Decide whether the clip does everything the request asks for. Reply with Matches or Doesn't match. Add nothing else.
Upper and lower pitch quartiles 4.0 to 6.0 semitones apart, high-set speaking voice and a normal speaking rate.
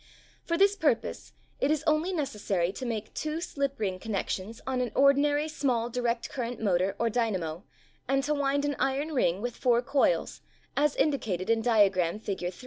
Matches